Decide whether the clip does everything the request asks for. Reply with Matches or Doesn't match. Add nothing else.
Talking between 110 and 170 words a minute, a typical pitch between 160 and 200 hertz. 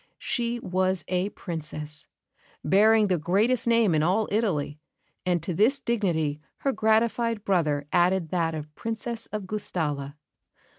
Matches